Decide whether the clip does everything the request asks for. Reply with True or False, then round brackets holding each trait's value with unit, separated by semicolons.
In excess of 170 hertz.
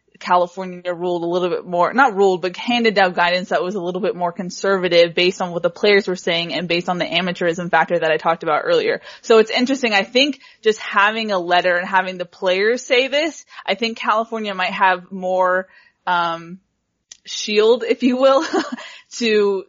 True (190 Hz)